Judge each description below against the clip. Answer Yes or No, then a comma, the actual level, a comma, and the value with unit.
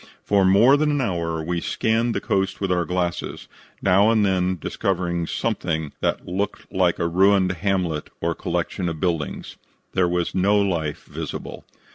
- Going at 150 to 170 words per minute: Yes, average, 160 wpm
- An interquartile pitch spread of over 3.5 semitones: No, average, 2.7 semitones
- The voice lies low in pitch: Yes, very low, 90 Hz